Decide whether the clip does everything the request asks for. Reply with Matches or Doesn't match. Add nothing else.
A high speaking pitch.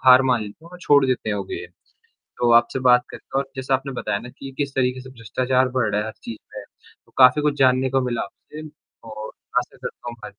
Doesn't match